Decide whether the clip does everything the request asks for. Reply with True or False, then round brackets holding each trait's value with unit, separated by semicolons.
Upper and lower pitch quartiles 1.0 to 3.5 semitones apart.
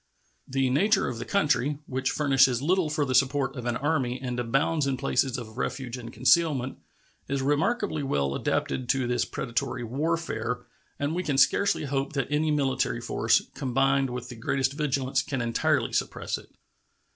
True (2.9 semitones)